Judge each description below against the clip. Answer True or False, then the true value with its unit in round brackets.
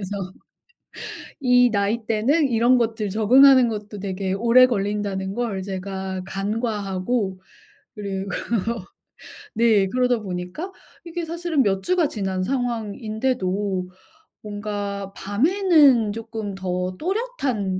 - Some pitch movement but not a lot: True (4.3 semitones)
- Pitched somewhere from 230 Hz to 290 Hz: False (215 Hz)